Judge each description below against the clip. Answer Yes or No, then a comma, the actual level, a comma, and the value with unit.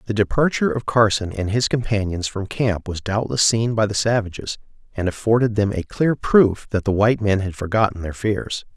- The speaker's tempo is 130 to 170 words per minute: No, average, 200 wpm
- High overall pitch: No, low, 105 Hz